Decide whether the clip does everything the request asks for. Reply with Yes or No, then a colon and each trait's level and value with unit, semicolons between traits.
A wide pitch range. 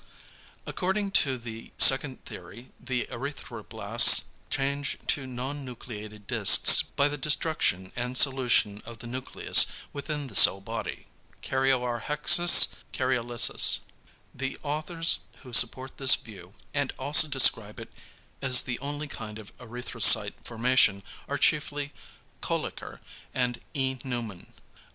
No: average, 3.4 semitones